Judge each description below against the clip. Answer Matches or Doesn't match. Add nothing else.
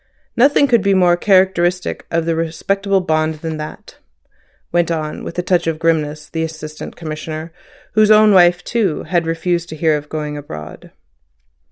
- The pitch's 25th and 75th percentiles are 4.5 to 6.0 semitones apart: Doesn't match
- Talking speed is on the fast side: Doesn't match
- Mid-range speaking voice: Matches